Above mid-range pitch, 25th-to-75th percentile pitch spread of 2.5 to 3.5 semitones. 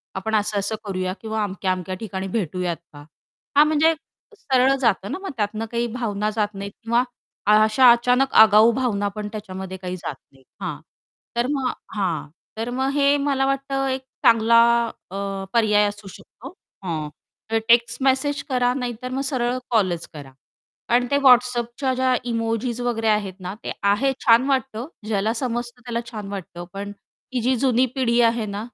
No: high, 230 Hz; average, 3.9 semitones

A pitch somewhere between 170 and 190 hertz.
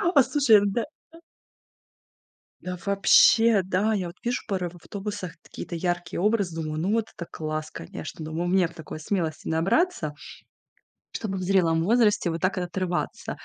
Yes: medium, 185 Hz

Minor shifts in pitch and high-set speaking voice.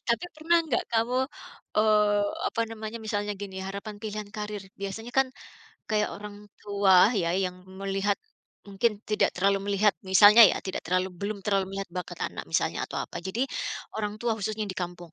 Yes: narrow, 1.7 semitones; high, 205 Hz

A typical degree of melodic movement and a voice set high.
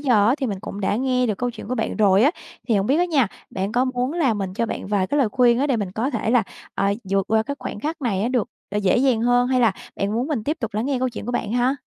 Yes: average, 3.7 semitones; high, 240 Hz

